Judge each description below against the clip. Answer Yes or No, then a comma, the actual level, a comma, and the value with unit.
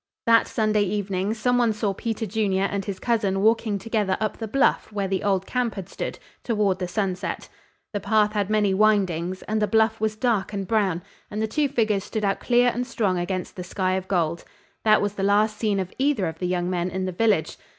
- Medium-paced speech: No, fast, 220 wpm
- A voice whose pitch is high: Yes, high, 205 Hz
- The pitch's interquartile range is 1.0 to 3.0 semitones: Yes, narrow, 2.6 semitones